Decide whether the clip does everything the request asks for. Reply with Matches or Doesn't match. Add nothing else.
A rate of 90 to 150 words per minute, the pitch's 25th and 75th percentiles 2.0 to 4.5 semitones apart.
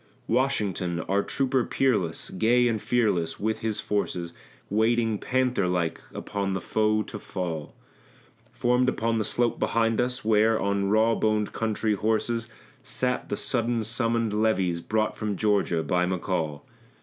Matches